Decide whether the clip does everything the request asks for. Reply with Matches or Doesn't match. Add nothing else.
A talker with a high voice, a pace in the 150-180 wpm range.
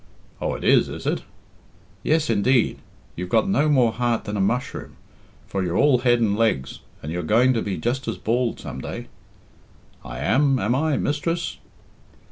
Doesn't match